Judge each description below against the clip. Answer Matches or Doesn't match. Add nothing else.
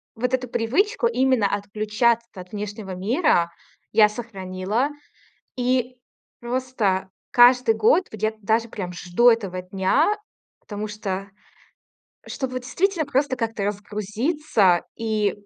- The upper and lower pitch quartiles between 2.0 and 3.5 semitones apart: Doesn't match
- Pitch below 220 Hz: Doesn't match